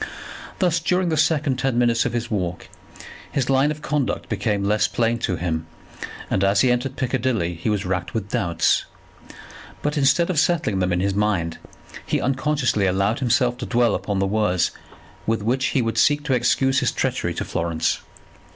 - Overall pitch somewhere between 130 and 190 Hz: No, low, 115 Hz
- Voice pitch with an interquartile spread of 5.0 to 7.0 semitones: Yes, wide, 5.6 semitones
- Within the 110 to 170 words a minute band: No, average, 180 wpm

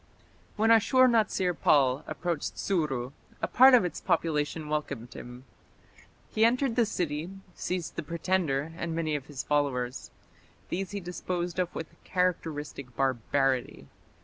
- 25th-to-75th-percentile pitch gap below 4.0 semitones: No, average, 4.8 semitones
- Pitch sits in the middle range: Yes, medium, 165 Hz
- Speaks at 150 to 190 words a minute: No, slow, 135 wpm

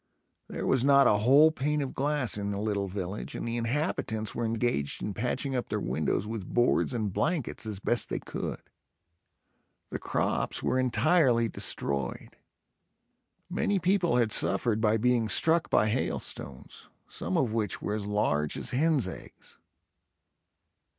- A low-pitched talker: Yes, low, 115 Hz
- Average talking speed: Yes, average, 150 wpm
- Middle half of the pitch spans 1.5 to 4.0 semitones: No, average, 4.6 semitones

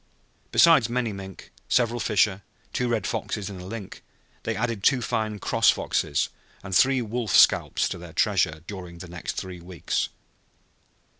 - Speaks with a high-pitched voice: No, low, 105 Hz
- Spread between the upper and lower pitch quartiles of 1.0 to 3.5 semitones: No, average, 4.4 semitones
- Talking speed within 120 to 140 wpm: No, average, 155 wpm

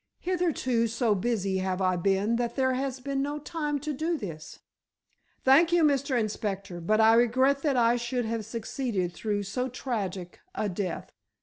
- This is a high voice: Yes, high, 235 Hz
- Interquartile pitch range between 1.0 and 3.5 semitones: No, average, 5.2 semitones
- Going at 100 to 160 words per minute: No, average, 170 wpm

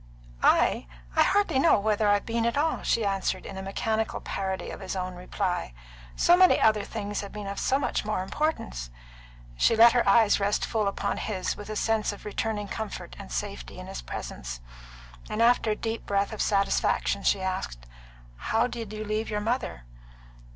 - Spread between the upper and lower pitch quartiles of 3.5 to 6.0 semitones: No, narrow, 2.6 semitones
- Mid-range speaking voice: No, high, 210 Hz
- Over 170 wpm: Yes, average, 185 wpm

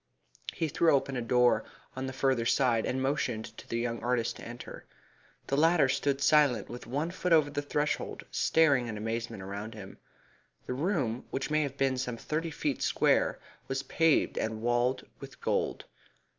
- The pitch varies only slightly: No, average, 3.7 semitones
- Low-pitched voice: Yes, low, 130 Hz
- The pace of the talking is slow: No, average, 175 wpm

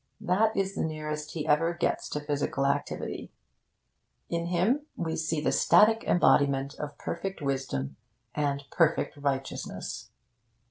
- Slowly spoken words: Yes, slow, 130 wpm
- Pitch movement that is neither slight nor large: Yes, average, 3.6 semitones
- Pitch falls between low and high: Yes, medium, 150 Hz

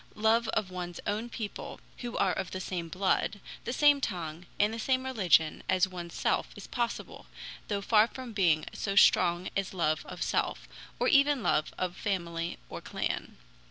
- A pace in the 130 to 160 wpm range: No, average, 175 wpm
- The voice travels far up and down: No, average, 4.7 semitones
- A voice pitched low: No, high, 195 Hz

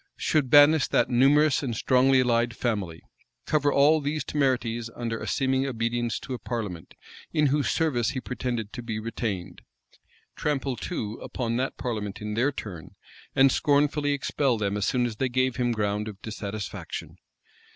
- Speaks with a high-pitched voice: No, low, 125 Hz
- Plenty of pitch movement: No, average, 3.6 semitones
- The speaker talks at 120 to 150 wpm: No, average, 160 wpm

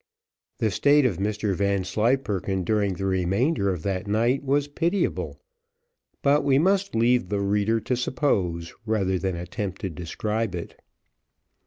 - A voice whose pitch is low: Yes, low, 105 Hz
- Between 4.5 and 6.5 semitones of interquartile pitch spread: Yes, average, 4.9 semitones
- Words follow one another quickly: No, average, 140 wpm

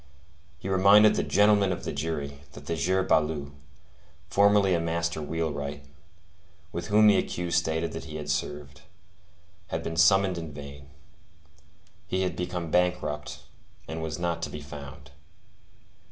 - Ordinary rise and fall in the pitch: Yes, average, 3.9 semitones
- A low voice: Yes, very low, 80 Hz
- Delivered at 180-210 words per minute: No, average, 145 wpm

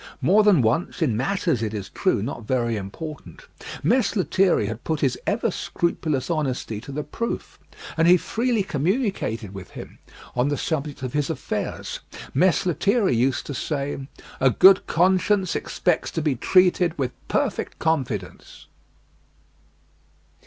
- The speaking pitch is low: No, medium, 155 Hz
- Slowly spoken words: No, average, 145 wpm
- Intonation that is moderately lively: No, wide, 6.7 semitones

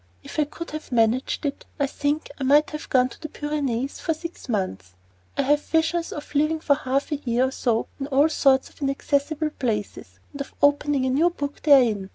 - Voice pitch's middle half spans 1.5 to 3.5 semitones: Yes, average, 2.7 semitones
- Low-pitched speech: No, very high, 280 Hz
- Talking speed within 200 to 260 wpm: Yes, fast, 205 wpm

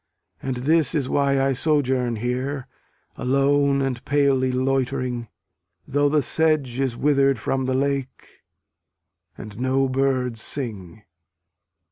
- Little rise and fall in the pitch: Yes, narrow, 1.9 semitones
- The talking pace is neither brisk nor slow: No, slow, 115 wpm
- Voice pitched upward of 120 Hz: Yes, low, 135 Hz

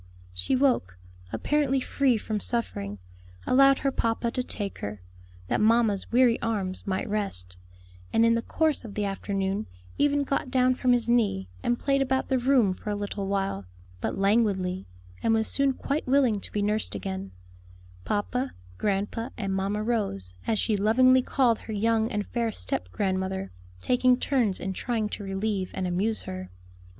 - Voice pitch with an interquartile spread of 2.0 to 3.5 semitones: No, average, 4.4 semitones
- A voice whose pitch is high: Yes, high, 215 Hz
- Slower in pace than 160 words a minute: No, average, 165 wpm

